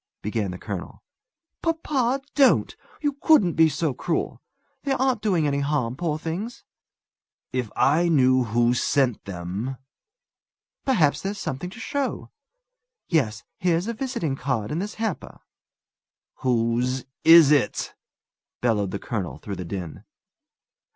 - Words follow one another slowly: Yes, slow, 130 wpm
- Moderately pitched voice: Yes, medium, 145 Hz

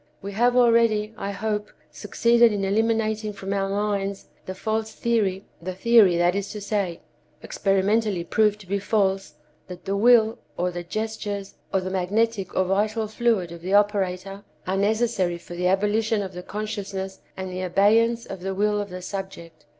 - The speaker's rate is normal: Yes, average, 165 wpm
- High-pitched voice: Yes, high, 200 Hz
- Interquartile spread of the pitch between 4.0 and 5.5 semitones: No, narrow, 2.4 semitones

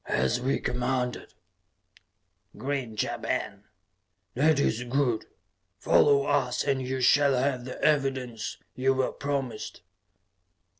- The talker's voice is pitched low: Yes, low, 130 Hz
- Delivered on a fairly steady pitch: Yes, narrow, 2.2 semitones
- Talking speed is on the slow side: Yes, slow, 110 wpm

